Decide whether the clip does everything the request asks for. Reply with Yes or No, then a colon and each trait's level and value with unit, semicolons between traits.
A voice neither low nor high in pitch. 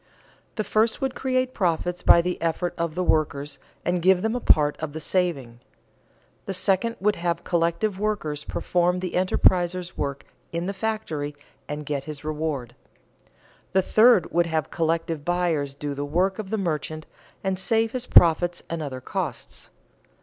Yes: medium, 175 Hz